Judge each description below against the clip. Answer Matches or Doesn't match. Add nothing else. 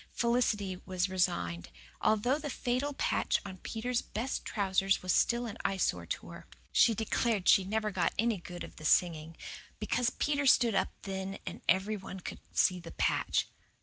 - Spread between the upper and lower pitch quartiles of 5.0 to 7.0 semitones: Doesn't match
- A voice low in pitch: Doesn't match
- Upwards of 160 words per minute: Matches